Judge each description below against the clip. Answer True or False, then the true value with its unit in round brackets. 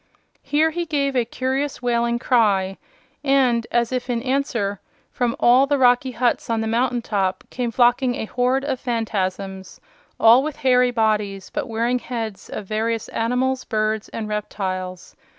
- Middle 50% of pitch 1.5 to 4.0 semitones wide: True (3.1 semitones)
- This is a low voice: False (240 Hz)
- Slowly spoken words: False (155 wpm)